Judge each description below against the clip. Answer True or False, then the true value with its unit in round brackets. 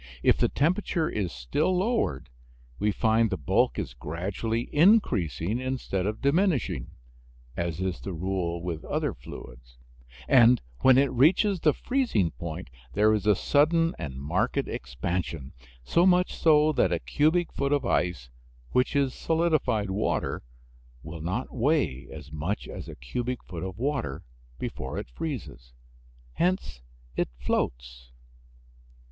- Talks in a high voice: False (105 Hz)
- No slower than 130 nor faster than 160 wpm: True (140 wpm)